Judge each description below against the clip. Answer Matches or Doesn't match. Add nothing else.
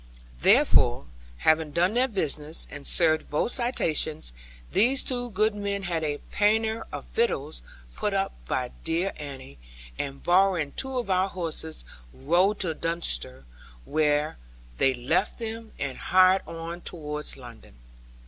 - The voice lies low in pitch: Doesn't match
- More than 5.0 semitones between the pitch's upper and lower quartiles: Matches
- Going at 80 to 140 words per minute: Matches